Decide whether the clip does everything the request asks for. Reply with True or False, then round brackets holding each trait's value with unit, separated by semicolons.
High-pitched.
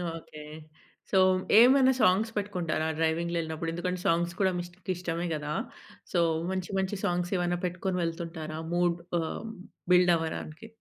False (175 Hz)